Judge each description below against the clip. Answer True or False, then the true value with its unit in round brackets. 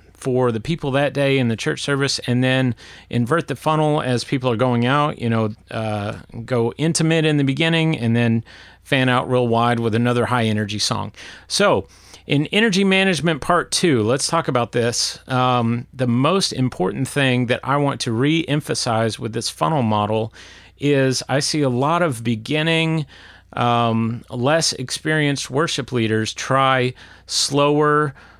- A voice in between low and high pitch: False (130 Hz)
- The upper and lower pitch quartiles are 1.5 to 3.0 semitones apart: False (4.1 semitones)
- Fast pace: False (165 wpm)